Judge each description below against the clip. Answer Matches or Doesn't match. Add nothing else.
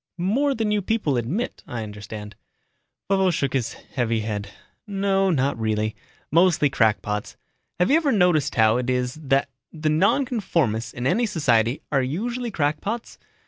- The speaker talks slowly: Doesn't match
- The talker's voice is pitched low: Doesn't match